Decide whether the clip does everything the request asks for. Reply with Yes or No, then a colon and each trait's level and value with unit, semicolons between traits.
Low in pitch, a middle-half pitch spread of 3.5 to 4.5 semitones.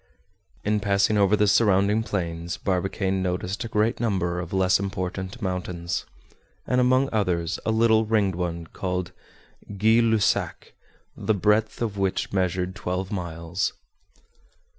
No: very low, 95 Hz; average, 2.8 semitones